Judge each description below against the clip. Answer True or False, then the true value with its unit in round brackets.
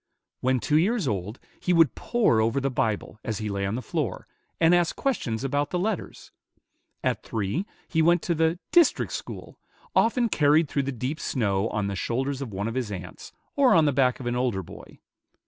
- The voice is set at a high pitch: False (135 Hz)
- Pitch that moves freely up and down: True (6.8 semitones)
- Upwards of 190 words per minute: True (200 wpm)